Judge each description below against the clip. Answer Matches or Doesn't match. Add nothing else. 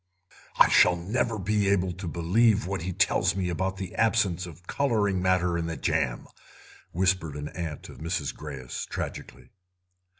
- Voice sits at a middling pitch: Doesn't match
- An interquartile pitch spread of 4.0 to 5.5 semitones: Doesn't match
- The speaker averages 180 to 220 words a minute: Doesn't match